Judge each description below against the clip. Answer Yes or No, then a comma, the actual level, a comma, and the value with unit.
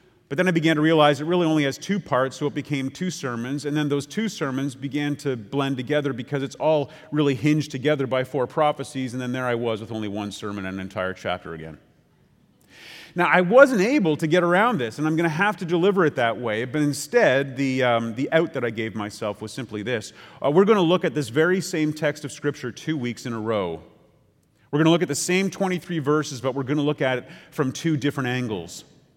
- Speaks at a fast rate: Yes, fast, 240 wpm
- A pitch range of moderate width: Yes, average, 4.1 semitones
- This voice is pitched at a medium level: Yes, medium, 145 Hz